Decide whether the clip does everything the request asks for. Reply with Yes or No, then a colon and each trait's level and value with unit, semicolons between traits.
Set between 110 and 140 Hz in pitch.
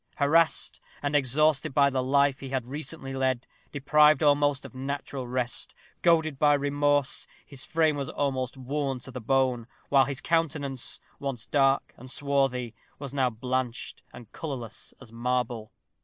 Yes: low, 135 Hz